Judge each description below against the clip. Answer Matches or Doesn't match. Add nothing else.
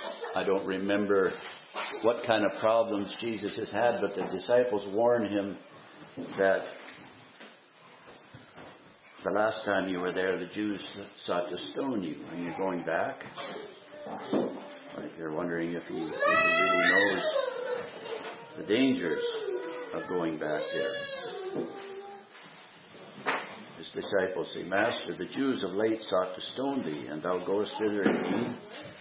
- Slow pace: Matches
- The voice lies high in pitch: Doesn't match